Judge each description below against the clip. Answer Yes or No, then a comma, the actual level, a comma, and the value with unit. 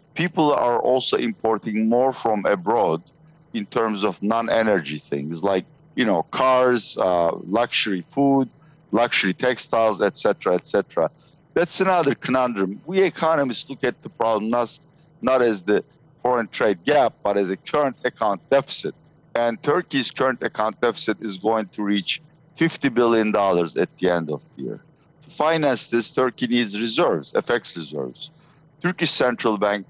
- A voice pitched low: Yes, low, 120 Hz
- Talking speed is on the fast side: No, average, 155 wpm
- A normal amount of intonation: No, wide, 6.4 semitones